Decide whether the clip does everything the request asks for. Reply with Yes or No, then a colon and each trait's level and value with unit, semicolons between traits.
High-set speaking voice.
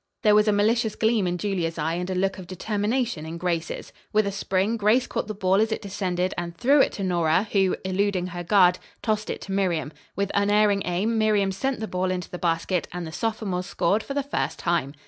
Yes: high, 195 Hz